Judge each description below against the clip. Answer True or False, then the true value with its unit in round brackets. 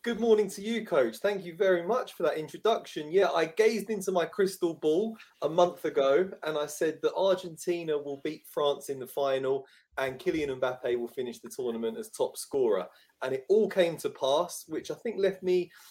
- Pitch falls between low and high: True (180 Hz)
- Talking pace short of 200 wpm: False (205 wpm)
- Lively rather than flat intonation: True (5.9 semitones)